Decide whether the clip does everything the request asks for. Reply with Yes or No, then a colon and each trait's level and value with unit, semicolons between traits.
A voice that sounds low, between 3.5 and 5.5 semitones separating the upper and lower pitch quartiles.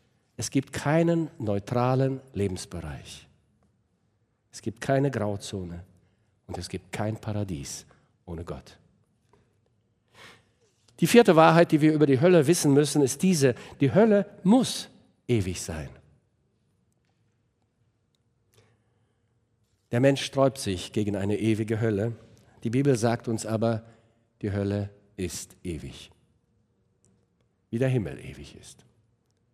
Yes: low, 115 Hz; average, 4.5 semitones